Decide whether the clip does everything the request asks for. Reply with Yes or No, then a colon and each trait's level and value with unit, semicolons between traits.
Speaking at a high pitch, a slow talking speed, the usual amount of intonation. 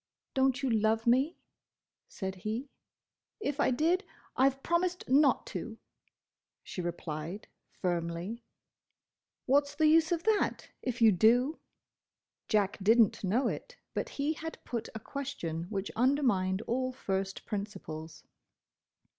No: high, 235 Hz; slow, 130 wpm; wide, 6.5 semitones